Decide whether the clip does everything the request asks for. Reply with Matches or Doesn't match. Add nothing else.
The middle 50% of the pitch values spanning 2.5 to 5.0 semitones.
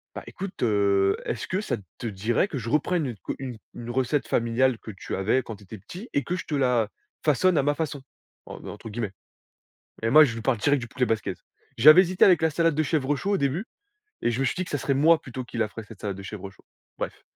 Doesn't match